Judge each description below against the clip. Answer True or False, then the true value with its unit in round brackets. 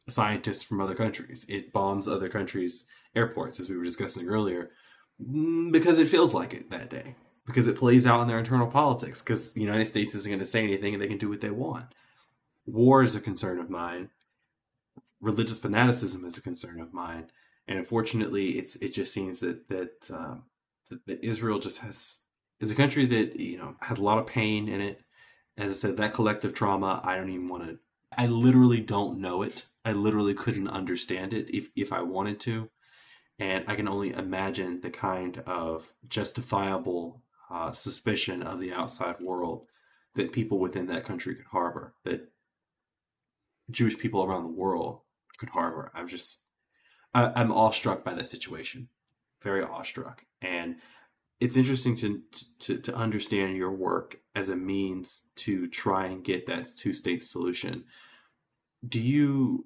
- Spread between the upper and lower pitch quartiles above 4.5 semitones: False (4.0 semitones)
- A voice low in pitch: True (105 Hz)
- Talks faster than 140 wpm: True (175 wpm)